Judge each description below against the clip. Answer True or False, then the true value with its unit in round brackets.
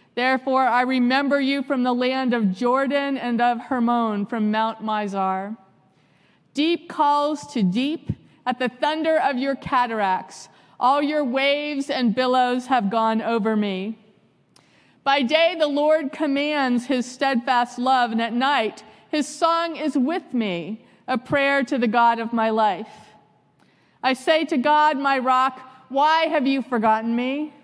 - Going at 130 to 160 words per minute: True (150 wpm)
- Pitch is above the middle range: True (255 Hz)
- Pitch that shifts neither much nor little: True (3.8 semitones)